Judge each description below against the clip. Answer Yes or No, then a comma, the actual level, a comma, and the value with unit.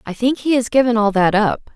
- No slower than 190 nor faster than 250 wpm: No, fast, 275 wpm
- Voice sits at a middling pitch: No, high, 230 Hz